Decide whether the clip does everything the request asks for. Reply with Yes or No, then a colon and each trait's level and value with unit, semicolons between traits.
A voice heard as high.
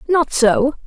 Yes: very high, 260 Hz